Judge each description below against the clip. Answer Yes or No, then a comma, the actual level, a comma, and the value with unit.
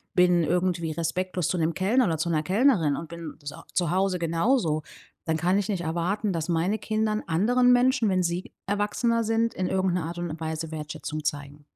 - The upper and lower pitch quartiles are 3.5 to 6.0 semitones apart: Yes, average, 4.1 semitones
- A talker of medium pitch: Yes, medium, 175 Hz